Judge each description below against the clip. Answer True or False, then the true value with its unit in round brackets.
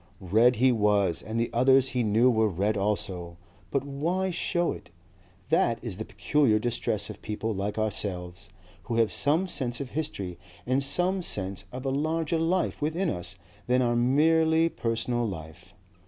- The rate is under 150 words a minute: False (165 wpm)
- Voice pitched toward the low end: True (120 Hz)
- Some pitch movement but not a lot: False (6.0 semitones)